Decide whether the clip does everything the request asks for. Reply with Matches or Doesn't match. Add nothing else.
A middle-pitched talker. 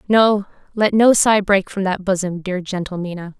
Doesn't match